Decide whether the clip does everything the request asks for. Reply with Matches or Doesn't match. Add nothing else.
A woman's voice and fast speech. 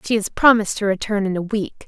Matches